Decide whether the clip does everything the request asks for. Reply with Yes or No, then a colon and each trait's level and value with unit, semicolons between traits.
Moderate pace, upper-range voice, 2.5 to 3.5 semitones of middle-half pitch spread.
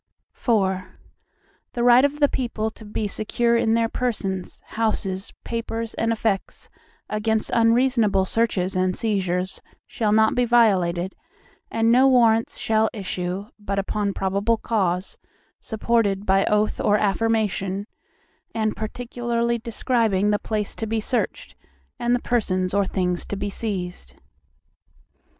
No: slow, 130 wpm; high, 215 Hz; average, 3.0 semitones